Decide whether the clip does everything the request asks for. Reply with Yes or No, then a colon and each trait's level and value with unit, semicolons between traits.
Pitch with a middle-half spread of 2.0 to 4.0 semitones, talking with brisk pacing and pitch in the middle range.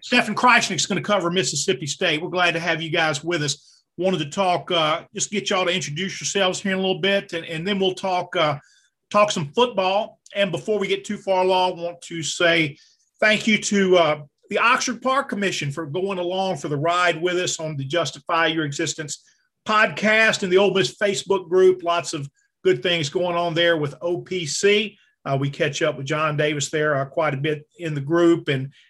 Yes: average, 3.4 semitones; fast, 215 wpm; medium, 175 Hz